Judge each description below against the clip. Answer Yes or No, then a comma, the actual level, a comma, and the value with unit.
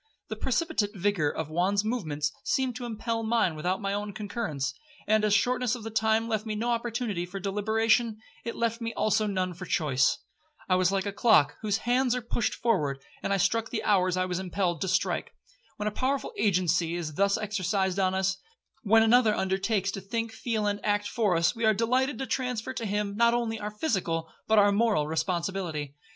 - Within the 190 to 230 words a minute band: Yes, average, 200 wpm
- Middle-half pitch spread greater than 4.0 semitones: No, average, 3.7 semitones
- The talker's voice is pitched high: Yes, high, 210 Hz